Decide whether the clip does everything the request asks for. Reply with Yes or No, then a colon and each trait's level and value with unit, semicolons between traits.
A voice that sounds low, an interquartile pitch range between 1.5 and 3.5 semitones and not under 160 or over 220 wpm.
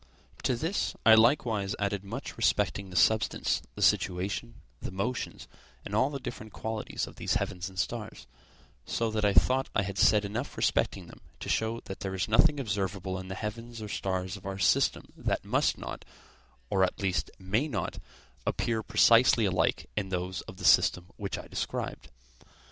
Yes: low, 100 Hz; average, 3.1 semitones; average, 175 wpm